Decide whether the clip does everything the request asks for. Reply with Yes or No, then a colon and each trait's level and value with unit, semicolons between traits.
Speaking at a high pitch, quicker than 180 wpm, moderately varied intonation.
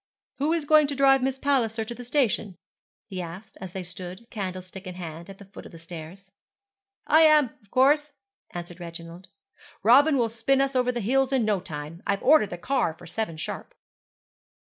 No: high, 215 Hz; average, 190 wpm; wide, 7.2 semitones